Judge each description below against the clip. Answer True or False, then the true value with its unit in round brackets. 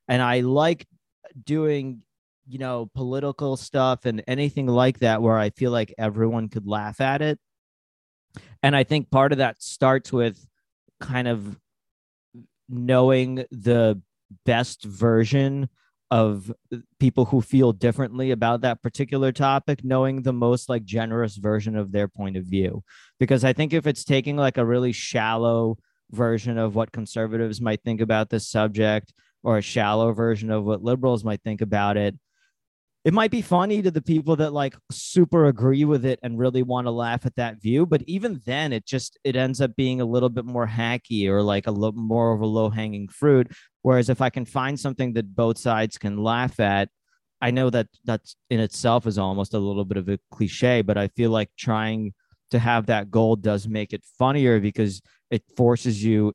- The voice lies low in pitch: True (120 Hz)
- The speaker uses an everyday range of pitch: True (3.1 semitones)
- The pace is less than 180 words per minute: False (185 wpm)